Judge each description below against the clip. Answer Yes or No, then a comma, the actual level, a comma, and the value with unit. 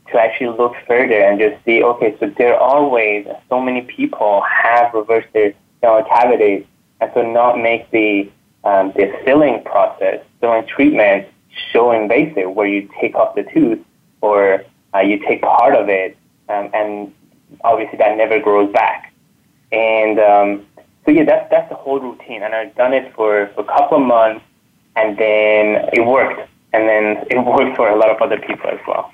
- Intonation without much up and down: No, average, 3.0 semitones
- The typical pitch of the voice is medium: No, low, 110 Hz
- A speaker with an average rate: Yes, average, 180 wpm